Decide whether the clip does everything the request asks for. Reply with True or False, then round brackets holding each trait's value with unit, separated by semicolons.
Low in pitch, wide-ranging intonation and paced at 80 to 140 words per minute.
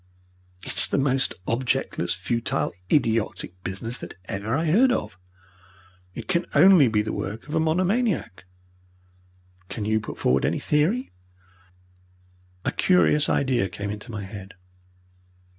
True (120 Hz; 7.4 semitones; 135 wpm)